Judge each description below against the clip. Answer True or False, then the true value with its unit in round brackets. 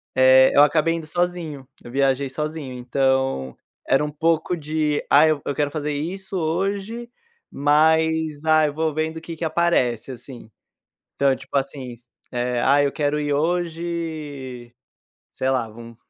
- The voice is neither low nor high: True (150 Hz)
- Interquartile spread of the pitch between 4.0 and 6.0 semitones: False (3.4 semitones)